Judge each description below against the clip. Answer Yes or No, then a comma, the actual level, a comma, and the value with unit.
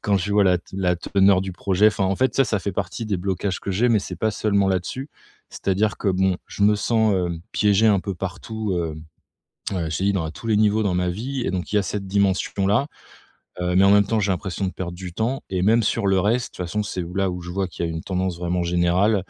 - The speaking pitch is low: Yes, very low, 95 Hz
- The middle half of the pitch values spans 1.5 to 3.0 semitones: Yes, narrow, 2.6 semitones